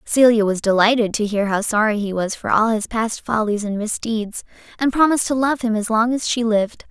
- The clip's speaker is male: No, female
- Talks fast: Yes, fast, 225 wpm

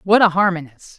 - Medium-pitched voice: Yes, medium, 180 Hz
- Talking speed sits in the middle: Yes, average, 185 wpm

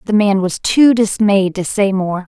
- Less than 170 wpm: No, fast, 205 wpm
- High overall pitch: Yes, high, 200 Hz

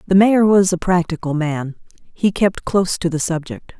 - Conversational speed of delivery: Yes, average, 190 wpm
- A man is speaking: No, female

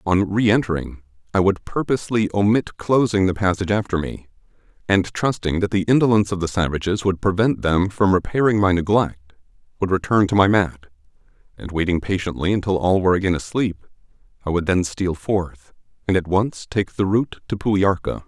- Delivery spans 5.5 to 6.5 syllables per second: Yes, 5.6 syllables/s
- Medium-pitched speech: No, very low, 95 Hz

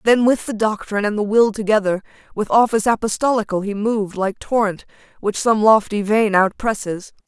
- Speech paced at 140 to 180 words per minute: Yes, average, 175 wpm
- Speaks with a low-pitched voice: No, high, 210 Hz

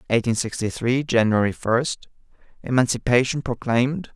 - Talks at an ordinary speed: No, slow, 85 wpm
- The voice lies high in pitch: No, low, 120 Hz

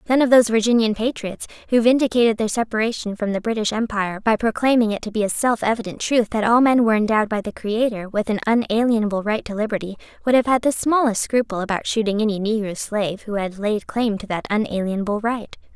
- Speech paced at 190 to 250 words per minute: Yes, fast, 205 wpm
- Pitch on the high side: Yes, high, 220 Hz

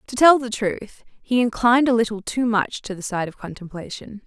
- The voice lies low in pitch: No, high, 220 Hz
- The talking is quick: Yes, fast, 210 wpm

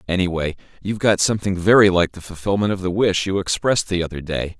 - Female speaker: No, male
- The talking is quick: Yes, fast, 220 wpm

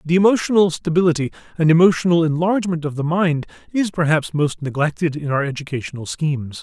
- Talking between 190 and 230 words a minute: No, average, 155 wpm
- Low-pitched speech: No, medium, 160 Hz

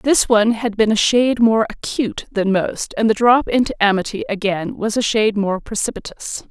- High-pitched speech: Yes, high, 220 Hz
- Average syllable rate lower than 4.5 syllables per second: No, 5.3 syllables/s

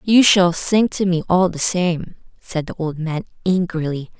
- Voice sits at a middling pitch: Yes, medium, 175 Hz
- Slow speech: No, average, 185 wpm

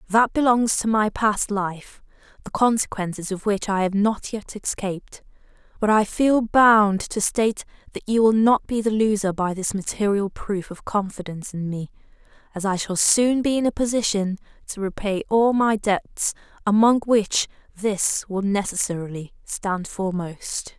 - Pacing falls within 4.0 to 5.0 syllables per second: Yes, 4.5 syllables/s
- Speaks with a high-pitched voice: Yes, high, 205 Hz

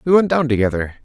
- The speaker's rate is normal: No, fast, 230 wpm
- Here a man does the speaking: Yes, male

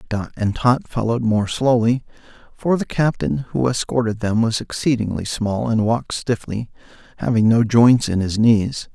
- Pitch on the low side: Yes, low, 115 Hz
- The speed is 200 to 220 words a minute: No, average, 160 wpm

